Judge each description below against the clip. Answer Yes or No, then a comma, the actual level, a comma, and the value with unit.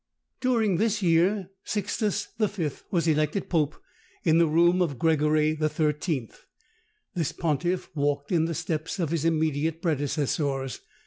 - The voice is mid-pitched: Yes, medium, 160 Hz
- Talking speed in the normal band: No, slow, 130 wpm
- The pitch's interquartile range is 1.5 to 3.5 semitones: Yes, average, 2.8 semitones